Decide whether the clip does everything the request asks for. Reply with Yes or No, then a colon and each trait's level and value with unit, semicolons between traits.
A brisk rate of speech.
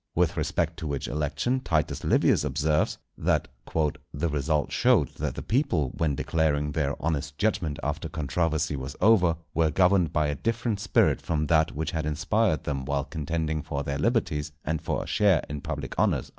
No: average, 175 wpm